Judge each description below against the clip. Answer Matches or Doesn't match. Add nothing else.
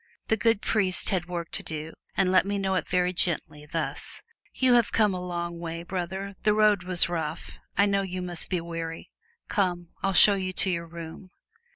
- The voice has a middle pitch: Matches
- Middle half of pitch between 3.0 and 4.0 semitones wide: Doesn't match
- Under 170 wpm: Doesn't match